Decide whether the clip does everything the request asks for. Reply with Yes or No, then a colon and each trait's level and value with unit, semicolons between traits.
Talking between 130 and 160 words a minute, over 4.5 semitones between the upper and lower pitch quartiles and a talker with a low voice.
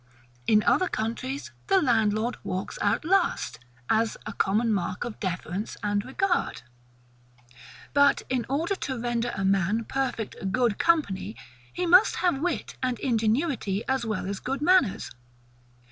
No: average, 140 wpm; wide, 5.6 semitones; high, 235 Hz